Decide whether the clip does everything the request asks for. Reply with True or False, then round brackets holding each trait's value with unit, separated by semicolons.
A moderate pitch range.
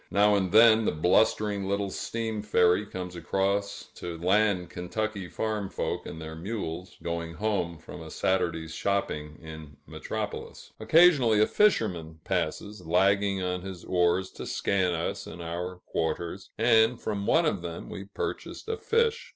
True (3.7 semitones)